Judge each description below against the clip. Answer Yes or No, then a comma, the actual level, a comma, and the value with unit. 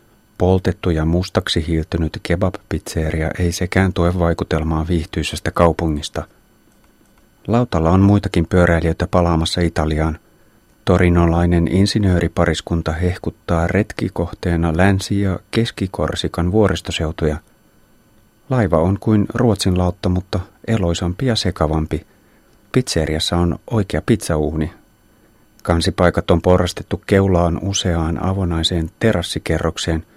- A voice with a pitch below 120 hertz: Yes, very low, 90 Hz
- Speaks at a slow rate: Yes, slow, 90 wpm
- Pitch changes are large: No, average, 3.5 semitones